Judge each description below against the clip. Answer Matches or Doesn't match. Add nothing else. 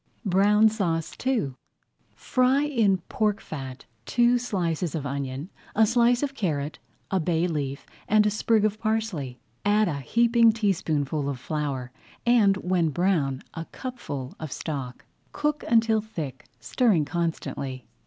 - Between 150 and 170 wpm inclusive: Doesn't match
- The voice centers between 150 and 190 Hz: Matches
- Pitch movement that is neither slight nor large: Doesn't match